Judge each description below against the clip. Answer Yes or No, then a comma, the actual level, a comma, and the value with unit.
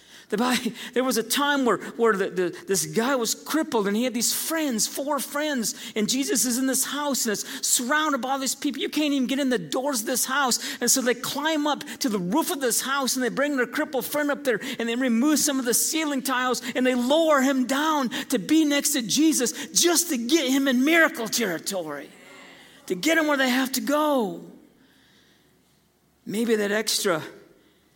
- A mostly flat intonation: No, average, 3.4 semitones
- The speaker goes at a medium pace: No, fast, 210 wpm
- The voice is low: No, very high, 265 Hz